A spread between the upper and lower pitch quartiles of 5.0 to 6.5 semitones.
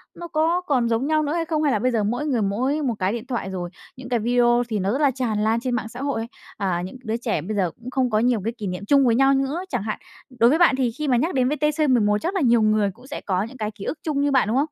No: average, 4.5 semitones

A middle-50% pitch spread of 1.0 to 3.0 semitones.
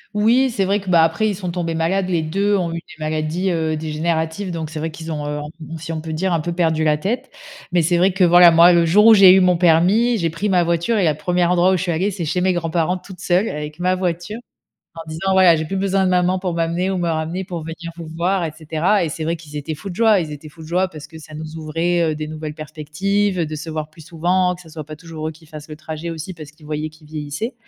Yes: average, 2.7 semitones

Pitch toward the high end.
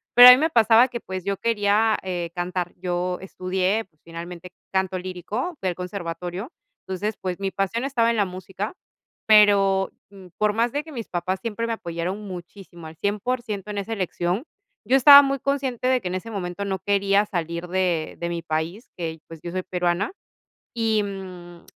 Yes: high, 195 Hz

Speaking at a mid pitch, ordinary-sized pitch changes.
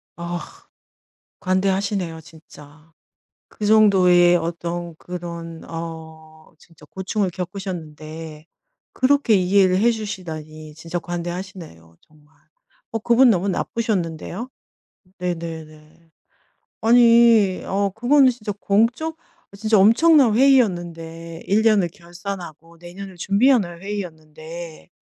Yes: medium, 180 Hz; average, 4.2 semitones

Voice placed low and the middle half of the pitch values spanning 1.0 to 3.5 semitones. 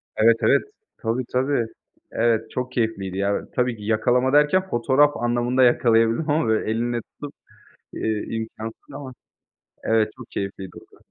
Yes: low, 120 Hz; narrow, 2.6 semitones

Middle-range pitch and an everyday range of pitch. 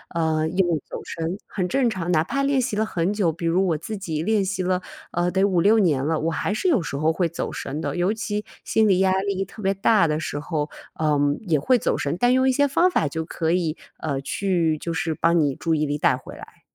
Yes: medium, 175 Hz; average, 4.2 semitones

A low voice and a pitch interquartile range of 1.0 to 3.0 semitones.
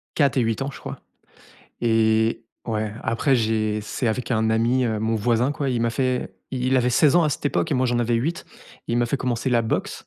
Yes: low, 120 Hz; narrow, 2.5 semitones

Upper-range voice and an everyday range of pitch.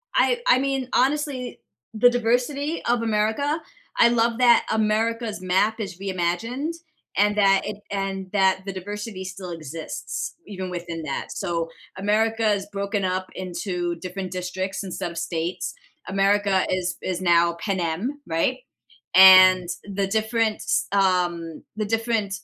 Yes: high, 195 Hz; average, 3.6 semitones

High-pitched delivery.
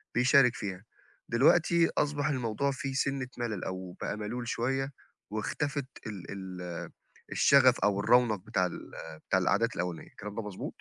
No: low, 115 Hz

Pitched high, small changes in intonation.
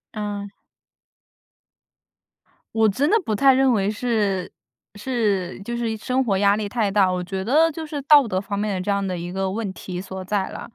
No: high, 205 Hz; average, 3.7 semitones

